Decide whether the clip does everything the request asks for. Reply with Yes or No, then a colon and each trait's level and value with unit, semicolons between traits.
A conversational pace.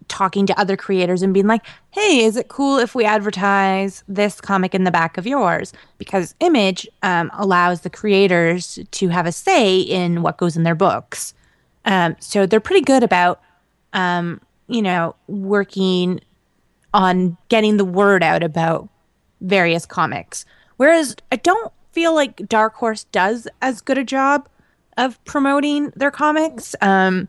Yes: average, 160 wpm